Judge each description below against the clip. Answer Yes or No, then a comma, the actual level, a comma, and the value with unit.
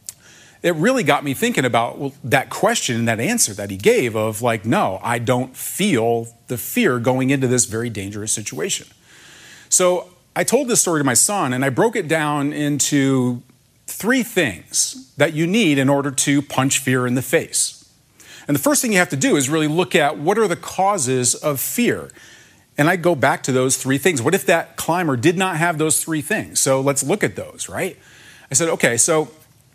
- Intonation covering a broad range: No, average, 4.9 semitones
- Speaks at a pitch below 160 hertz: Yes, medium, 140 Hz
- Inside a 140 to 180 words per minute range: No, fast, 205 wpm